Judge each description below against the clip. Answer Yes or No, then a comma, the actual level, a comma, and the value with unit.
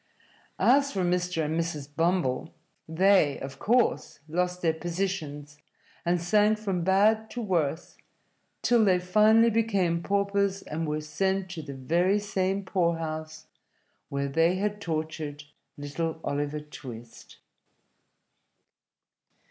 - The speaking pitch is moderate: Yes, medium, 175 Hz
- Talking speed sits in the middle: No, slow, 115 wpm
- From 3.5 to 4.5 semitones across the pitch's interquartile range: Yes, average, 4.2 semitones